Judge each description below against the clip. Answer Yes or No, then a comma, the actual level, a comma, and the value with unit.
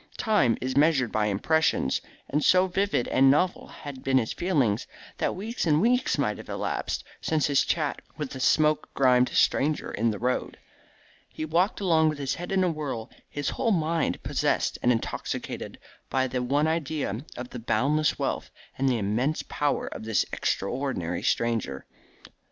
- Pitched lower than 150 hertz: Yes, medium, 140 Hz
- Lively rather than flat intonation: No, average, 4.3 semitones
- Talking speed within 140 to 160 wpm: No, average, 170 wpm